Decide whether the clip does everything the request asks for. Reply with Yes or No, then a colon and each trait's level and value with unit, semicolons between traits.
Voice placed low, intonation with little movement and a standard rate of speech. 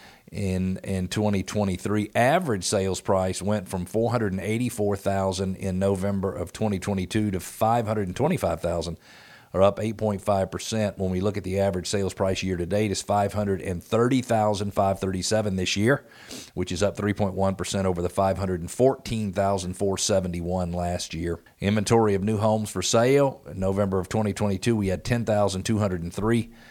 No: low, 100 Hz; narrow, 2.2 semitones; slow, 125 wpm